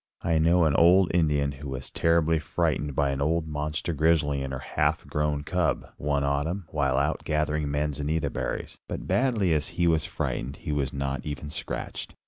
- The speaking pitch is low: Yes, very low, 75 Hz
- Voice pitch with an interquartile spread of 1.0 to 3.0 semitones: Yes, narrow, 2.5 semitones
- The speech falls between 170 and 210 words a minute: Yes, average, 180 wpm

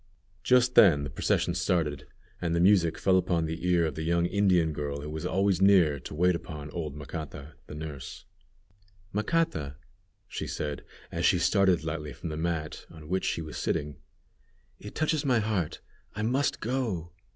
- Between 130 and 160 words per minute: No, average, 175 wpm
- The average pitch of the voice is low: Yes, very low, 85 Hz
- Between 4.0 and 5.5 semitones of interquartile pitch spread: Yes, average, 4.4 semitones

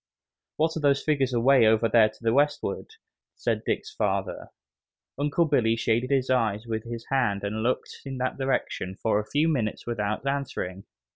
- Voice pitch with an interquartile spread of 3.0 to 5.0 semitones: Yes, average, 4.0 semitones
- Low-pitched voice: Yes, low, 120 Hz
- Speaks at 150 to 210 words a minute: Yes, average, 170 wpm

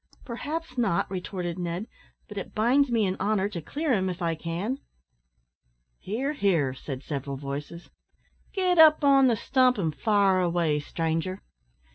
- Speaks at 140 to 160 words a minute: Yes, average, 150 wpm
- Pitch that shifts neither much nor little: No, wide, 7.1 semitones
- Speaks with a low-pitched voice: No, high, 190 Hz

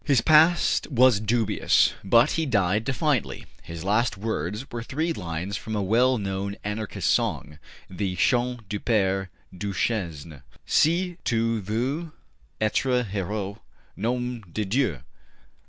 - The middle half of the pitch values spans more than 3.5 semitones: Yes, average, 4.5 semitones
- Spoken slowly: Yes, slow, 125 wpm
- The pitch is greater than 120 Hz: No, low, 110 Hz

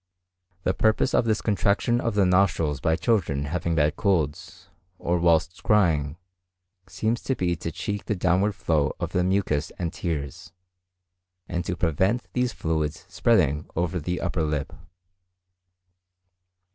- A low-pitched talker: Yes, very low, 90 Hz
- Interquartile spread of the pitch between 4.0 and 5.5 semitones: Yes, average, 4.3 semitones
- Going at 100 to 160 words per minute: Yes, average, 140 wpm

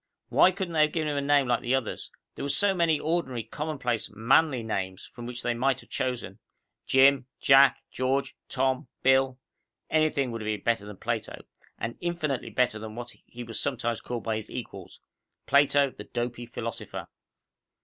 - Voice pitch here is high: No, low, 130 Hz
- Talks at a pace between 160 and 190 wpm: Yes, average, 180 wpm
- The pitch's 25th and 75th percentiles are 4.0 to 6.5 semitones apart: No, average, 3.3 semitones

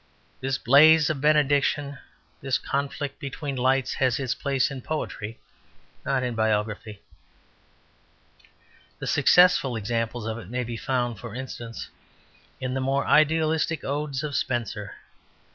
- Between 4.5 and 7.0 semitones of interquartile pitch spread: No, average, 3.5 semitones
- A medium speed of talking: No, slow, 125 wpm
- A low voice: Yes, low, 130 Hz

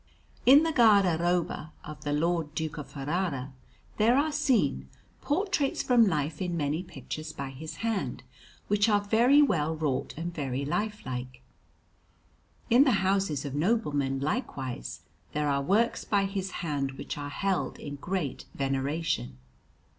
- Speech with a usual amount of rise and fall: No, wide, 6.6 semitones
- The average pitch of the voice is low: No, medium, 165 Hz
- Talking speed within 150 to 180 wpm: No, average, 140 wpm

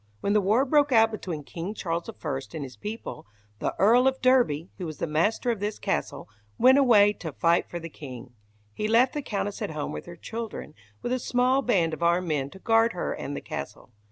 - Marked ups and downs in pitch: Yes, wide, 6.4 semitones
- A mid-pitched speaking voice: No, high, 200 Hz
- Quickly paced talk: Yes, fast, 220 wpm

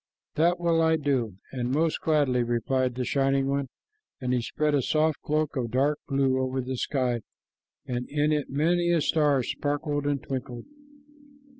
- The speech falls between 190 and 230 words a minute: No, average, 165 wpm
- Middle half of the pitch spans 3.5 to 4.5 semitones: No, average, 3.0 semitones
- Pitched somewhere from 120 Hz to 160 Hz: Yes, medium, 140 Hz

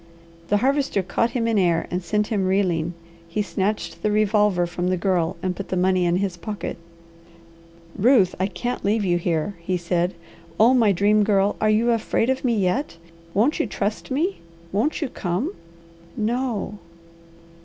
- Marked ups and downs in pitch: No, average, 3.8 semitones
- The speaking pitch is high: Yes, high, 200 Hz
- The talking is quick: No, average, 170 wpm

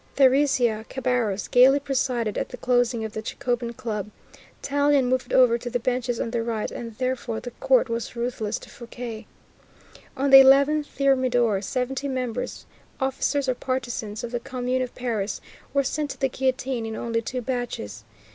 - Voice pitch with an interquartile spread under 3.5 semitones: Yes, narrow, 2.4 semitones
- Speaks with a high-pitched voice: Yes, very high, 250 Hz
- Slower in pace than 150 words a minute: No, average, 165 wpm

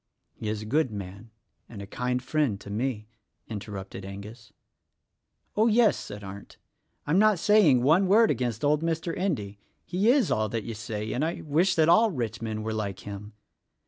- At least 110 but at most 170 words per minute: No, average, 180 wpm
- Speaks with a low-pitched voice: Yes, low, 120 Hz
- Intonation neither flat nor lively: No, wide, 7.9 semitones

